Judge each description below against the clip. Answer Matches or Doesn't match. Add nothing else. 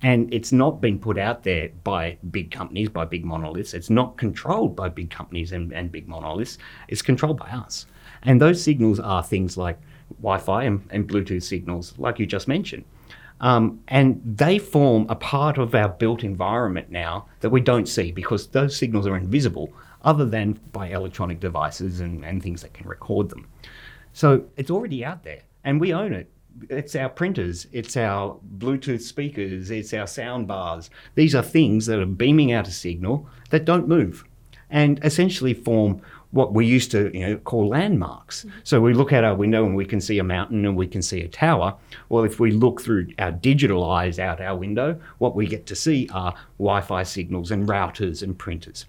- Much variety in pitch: Matches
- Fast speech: Doesn't match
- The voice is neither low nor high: Doesn't match